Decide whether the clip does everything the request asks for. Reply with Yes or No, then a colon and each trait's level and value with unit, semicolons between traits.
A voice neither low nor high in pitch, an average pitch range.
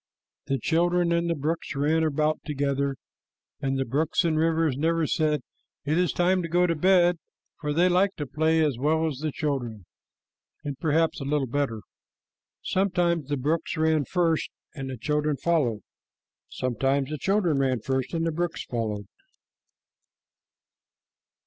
Yes: medium, 155 Hz; average, 3.4 semitones